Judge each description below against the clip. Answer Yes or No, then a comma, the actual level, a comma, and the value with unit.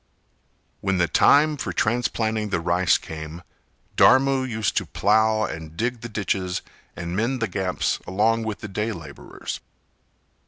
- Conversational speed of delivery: Yes, average, 145 wpm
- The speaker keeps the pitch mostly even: No, average, 4.1 semitones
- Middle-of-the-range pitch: No, low, 105 Hz